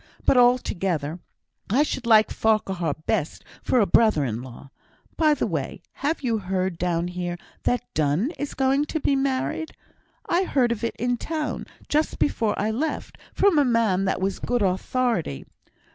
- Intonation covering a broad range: Yes, wide, 6.8 semitones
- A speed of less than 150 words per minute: No, average, 165 wpm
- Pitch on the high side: Yes, high, 225 Hz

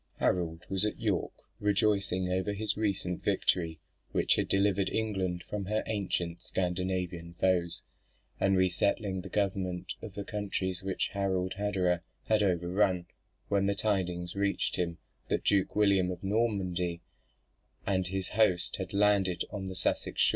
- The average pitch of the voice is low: Yes, very low, 95 Hz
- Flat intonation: Yes, narrow, 2.0 semitones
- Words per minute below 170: Yes, average, 145 wpm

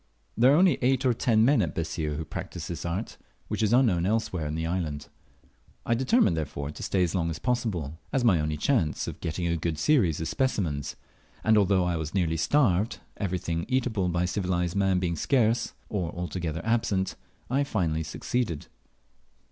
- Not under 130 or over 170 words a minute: No, average, 185 wpm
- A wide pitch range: Yes, wide, 5.8 semitones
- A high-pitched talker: No, very low, 90 Hz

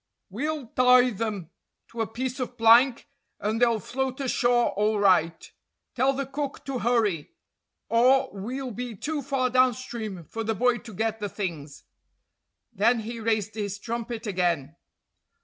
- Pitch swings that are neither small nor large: Yes, average, 3.4 semitones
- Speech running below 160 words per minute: Yes, average, 150 wpm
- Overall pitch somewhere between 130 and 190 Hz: No, high, 230 Hz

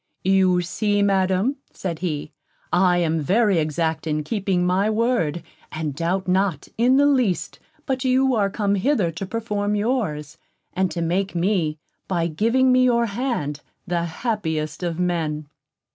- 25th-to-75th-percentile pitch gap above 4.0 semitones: Yes, average, 4.8 semitones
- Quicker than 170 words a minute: No, average, 150 wpm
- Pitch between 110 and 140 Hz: No, medium, 185 Hz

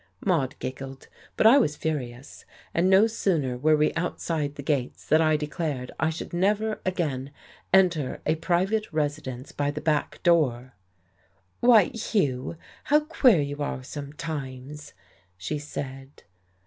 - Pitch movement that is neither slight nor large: Yes, average, 4.6 semitones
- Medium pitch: Yes, medium, 150 Hz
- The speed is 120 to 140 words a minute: Yes, slow, 135 wpm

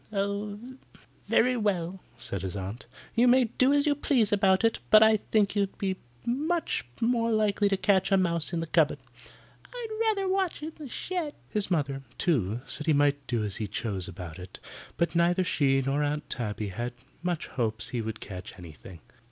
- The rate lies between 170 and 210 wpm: Yes, average, 185 wpm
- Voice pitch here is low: No, medium, 175 Hz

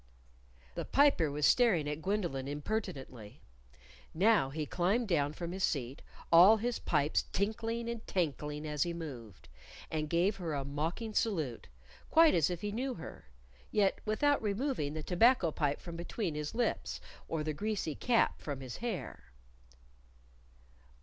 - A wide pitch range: Yes, wide, 6.7 semitones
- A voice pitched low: No, medium, 170 Hz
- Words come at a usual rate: Yes, average, 150 wpm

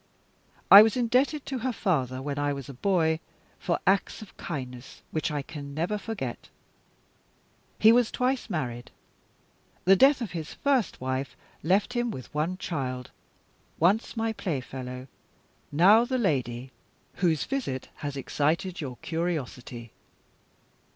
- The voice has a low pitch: No, medium, 165 Hz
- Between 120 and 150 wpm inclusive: Yes, slow, 135 wpm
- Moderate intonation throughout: No, wide, 8.4 semitones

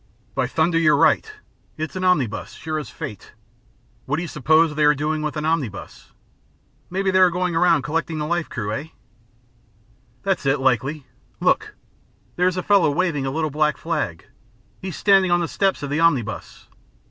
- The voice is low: No, medium, 155 Hz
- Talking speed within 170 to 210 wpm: Yes, average, 175 wpm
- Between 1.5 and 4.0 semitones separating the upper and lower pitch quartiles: Yes, average, 3.3 semitones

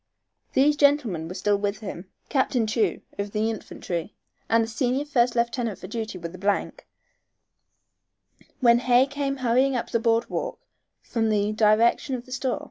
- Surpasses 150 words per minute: Yes, average, 165 wpm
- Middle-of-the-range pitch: No, high, 230 Hz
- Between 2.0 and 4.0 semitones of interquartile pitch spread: Yes, average, 3.7 semitones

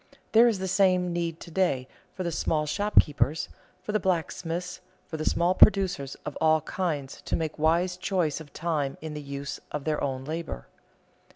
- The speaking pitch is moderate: Yes, medium, 165 Hz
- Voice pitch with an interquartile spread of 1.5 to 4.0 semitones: Yes, average, 3.5 semitones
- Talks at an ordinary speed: Yes, average, 180 wpm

